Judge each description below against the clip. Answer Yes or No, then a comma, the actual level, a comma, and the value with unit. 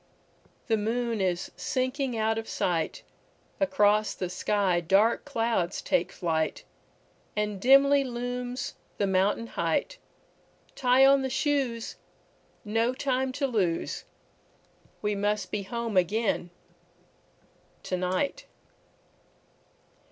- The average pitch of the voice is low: No, high, 225 Hz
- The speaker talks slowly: Yes, slow, 90 wpm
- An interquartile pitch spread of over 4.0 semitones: Yes, average, 4.8 semitones